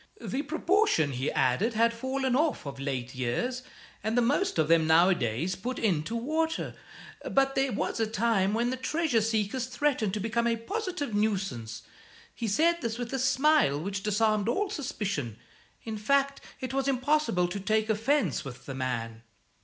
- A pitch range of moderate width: No, wide, 7.1 semitones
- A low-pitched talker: No, high, 225 Hz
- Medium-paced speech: Yes, average, 170 wpm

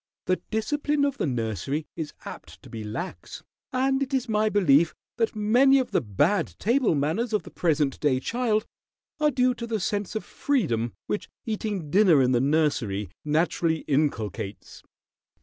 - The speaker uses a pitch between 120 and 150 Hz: No, medium, 185 Hz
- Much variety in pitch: Yes, wide, 8.9 semitones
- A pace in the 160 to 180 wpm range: Yes, average, 165 wpm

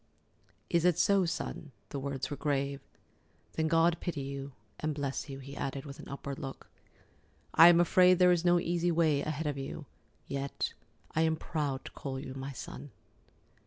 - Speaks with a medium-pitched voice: Yes, medium, 145 Hz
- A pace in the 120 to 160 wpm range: No, average, 170 wpm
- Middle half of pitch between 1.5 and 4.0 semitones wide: Yes, average, 3.3 semitones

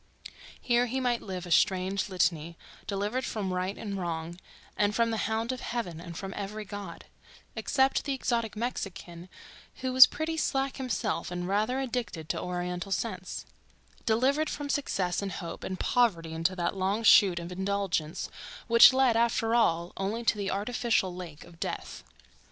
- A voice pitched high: Yes, high, 200 Hz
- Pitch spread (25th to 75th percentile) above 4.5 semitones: Yes, average, 4.9 semitones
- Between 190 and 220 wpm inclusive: No, average, 165 wpm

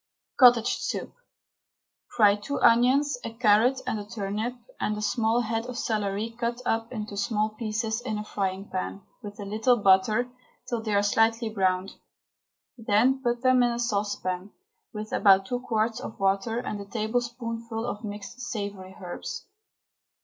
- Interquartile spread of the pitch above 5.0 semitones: No, average, 2.7 semitones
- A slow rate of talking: No, average, 155 wpm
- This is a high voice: Yes, high, 220 Hz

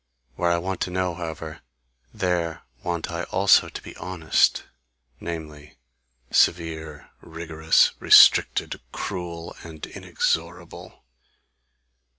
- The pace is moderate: No, slow, 100 wpm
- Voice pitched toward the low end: Yes, very low, 85 Hz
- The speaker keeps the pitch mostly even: Yes, narrow, 1.7 semitones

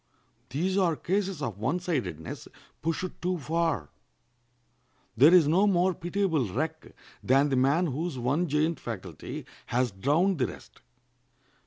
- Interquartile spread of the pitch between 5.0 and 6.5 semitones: Yes, wide, 5.5 semitones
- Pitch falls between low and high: Yes, medium, 155 Hz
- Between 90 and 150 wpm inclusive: Yes, slow, 135 wpm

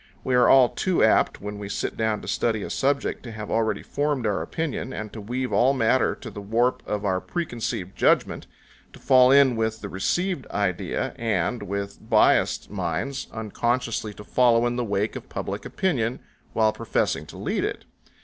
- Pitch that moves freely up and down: No, average, 3.7 semitones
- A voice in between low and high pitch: No, low, 115 Hz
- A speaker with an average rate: Yes, average, 185 wpm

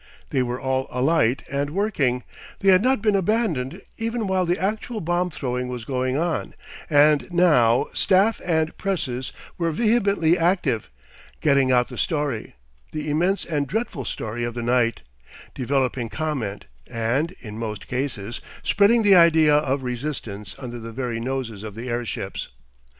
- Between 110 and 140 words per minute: No, average, 150 wpm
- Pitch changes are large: Yes, wide, 6.3 semitones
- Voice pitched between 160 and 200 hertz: No, medium, 140 Hz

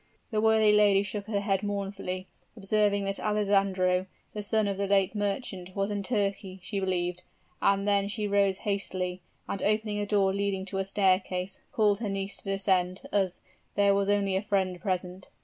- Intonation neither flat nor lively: No, narrow, 1.3 semitones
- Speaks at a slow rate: No, average, 180 wpm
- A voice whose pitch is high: Yes, high, 200 Hz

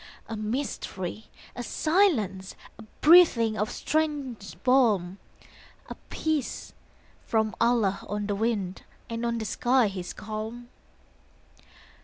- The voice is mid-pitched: No, high, 225 Hz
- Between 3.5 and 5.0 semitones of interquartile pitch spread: Yes, average, 3.8 semitones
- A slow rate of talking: Yes, slow, 110 wpm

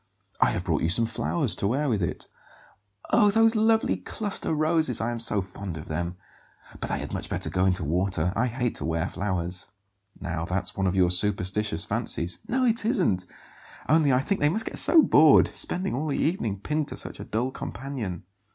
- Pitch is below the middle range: Yes, low, 115 Hz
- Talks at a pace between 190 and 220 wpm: Yes, average, 200 wpm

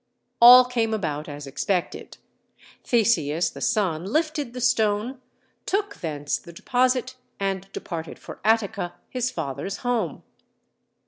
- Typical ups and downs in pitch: No, wide, 6.6 semitones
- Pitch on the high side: Yes, high, 215 Hz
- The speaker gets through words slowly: Yes, slow, 120 wpm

